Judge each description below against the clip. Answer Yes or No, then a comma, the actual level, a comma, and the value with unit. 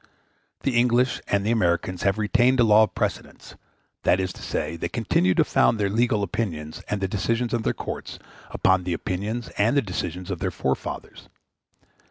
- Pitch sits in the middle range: No, low, 100 Hz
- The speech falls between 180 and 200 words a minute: Yes, average, 185 wpm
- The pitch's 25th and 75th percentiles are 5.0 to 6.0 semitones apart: No, average, 4.2 semitones